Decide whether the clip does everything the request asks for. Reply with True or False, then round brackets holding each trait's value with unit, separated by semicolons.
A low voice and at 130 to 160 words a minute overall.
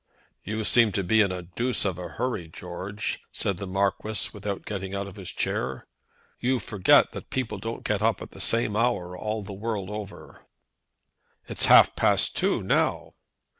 False (100 Hz; 175 wpm)